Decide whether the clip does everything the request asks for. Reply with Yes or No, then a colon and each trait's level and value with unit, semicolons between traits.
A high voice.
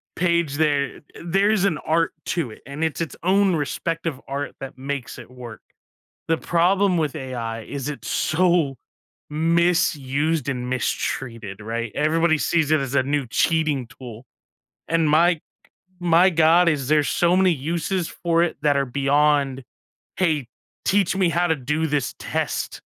No: medium, 155 Hz